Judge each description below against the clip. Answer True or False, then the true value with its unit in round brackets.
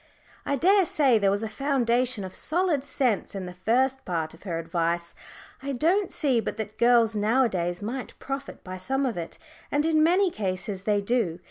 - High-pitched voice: True (235 Hz)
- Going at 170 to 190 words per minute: True (180 wpm)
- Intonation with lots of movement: True (6.5 semitones)